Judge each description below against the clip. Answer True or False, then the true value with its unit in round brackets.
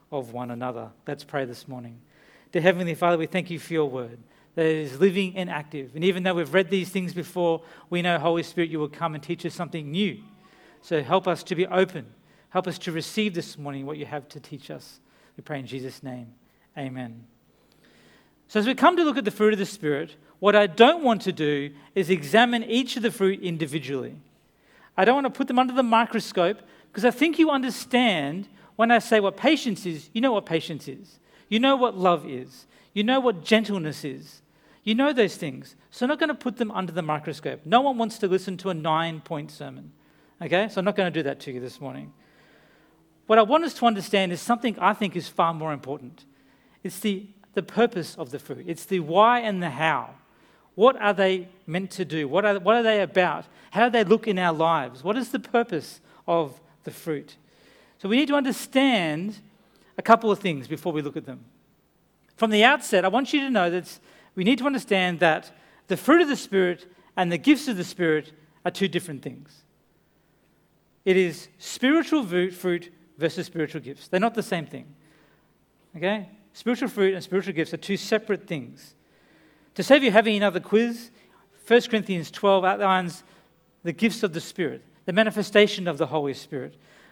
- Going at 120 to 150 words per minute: False (205 wpm)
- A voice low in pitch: False (185 Hz)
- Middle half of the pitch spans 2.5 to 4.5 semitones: False (5.2 semitones)